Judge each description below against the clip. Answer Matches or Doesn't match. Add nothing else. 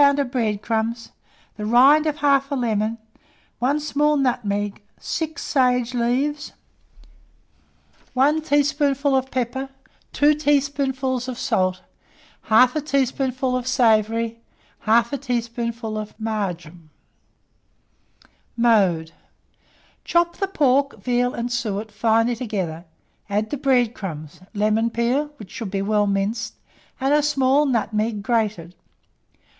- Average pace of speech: Doesn't match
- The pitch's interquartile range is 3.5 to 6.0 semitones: Matches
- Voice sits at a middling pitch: Doesn't match